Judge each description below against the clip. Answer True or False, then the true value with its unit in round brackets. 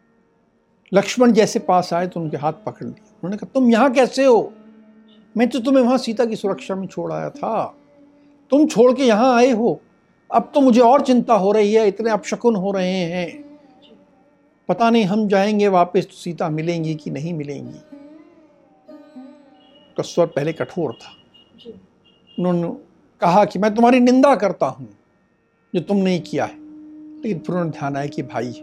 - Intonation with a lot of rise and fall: True (6.4 semitones)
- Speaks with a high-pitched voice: True (215 Hz)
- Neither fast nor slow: True (165 wpm)